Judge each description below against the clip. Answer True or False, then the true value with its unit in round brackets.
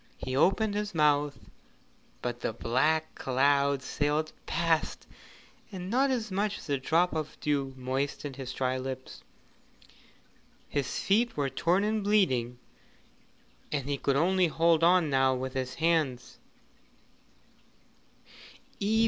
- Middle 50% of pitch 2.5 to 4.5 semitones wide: False (5.2 semitones)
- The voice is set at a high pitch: False (150 Hz)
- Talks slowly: True (125 wpm)